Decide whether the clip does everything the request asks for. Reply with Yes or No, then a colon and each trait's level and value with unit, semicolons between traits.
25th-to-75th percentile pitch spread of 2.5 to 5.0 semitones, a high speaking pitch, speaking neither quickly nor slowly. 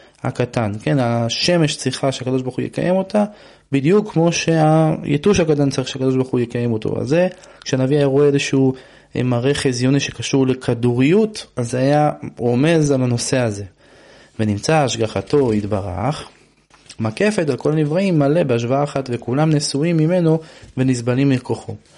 No: average, 4.1 semitones; low, 135 Hz; average, 140 wpm